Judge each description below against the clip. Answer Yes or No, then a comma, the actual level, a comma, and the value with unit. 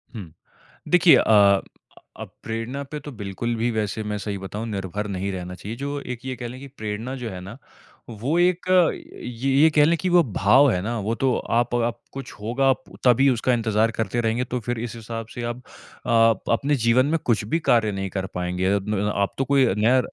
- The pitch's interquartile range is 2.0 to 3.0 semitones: No, average, 3.9 semitones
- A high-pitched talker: No, low, 115 Hz